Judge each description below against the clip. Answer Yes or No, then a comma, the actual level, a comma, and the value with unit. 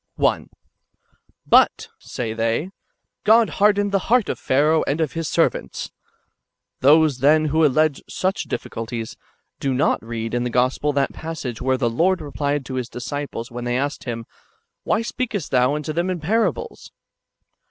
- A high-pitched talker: No, medium, 145 Hz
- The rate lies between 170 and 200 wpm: Yes, average, 175 wpm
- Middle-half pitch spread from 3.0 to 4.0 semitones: No, average, 5.0 semitones